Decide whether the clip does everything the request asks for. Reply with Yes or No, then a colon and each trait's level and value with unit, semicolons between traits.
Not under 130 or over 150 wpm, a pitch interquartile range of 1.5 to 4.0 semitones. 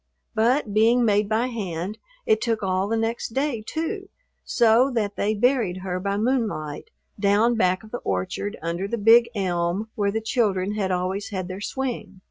No: average, 175 wpm; average, 3.6 semitones